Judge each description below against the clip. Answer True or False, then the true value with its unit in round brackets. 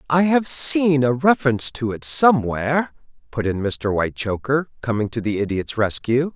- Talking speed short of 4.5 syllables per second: False (5.1 syllables/s)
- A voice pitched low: True (130 Hz)